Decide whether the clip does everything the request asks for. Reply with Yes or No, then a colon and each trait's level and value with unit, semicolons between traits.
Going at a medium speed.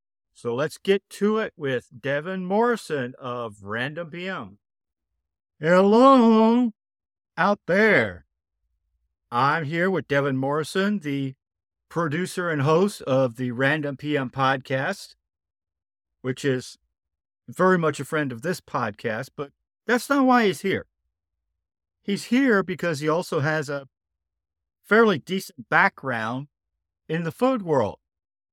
No: slow, 120 wpm